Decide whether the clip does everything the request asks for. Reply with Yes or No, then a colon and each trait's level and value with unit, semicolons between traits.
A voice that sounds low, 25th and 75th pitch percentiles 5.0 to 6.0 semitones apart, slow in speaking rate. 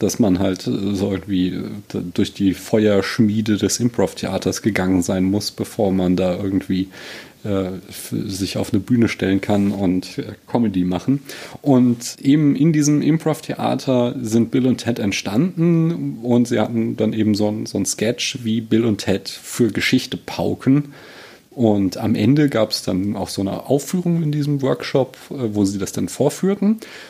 No: low, 110 Hz; average, 5.3 semitones; average, 155 wpm